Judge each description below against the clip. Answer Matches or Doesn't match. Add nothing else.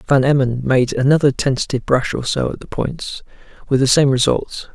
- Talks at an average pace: Matches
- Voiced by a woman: Doesn't match